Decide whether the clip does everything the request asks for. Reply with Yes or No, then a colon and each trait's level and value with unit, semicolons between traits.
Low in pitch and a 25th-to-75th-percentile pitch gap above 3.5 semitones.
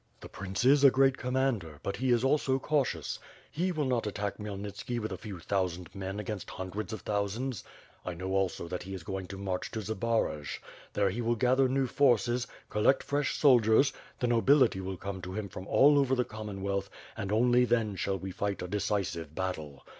Yes: low, 105 Hz; average, 4.6 semitones